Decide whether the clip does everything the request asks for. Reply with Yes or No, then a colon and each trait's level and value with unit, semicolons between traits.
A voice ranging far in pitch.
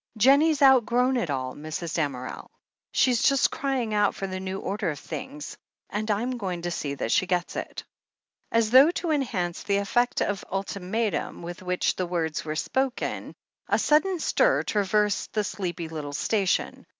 Yes: wide, 6.2 semitones